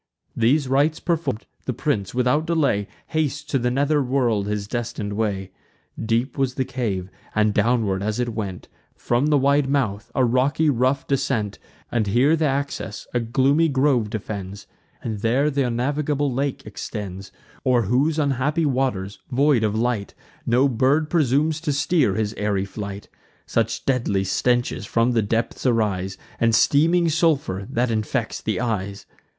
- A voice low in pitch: Yes, low, 125 Hz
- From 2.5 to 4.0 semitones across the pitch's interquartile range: No, average, 4.9 semitones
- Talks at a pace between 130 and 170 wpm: Yes, average, 155 wpm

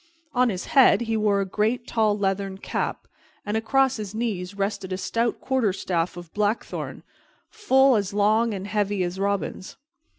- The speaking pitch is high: Yes, high, 210 Hz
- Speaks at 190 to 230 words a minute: No, average, 160 wpm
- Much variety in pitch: No, average, 3.1 semitones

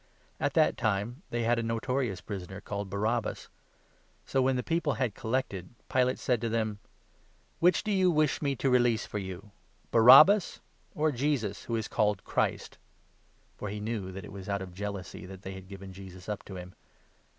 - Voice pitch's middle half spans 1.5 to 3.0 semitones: No, average, 4.7 semitones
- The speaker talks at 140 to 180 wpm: No, average, 195 wpm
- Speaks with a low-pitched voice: Yes, low, 110 Hz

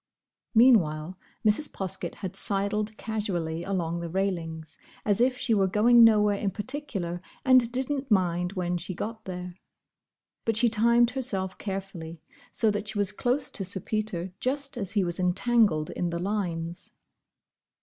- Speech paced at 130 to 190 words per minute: Yes, average, 150 wpm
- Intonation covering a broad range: No, average, 4.3 semitones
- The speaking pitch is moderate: No, high, 200 Hz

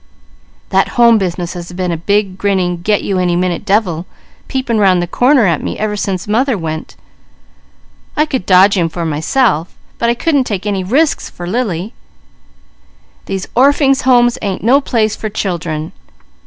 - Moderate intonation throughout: Yes, average, 5.0 semitones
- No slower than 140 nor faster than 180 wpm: Yes, average, 165 wpm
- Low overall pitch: No, high, 200 Hz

